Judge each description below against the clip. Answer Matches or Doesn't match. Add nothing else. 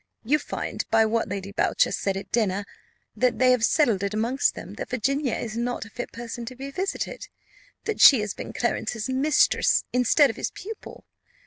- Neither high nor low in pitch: Doesn't match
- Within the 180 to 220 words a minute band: Matches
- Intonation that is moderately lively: Matches